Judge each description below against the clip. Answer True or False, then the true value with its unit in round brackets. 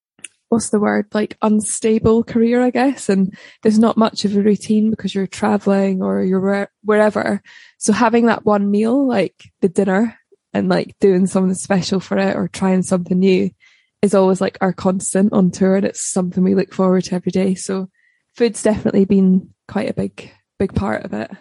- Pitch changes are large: False (2.4 semitones)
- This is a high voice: True (200 Hz)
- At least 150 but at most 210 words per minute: True (190 wpm)